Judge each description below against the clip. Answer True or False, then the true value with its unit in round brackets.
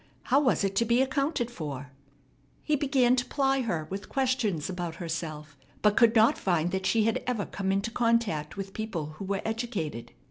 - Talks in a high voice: True (205 Hz)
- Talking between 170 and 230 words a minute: True (185 wpm)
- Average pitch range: False (6.3 semitones)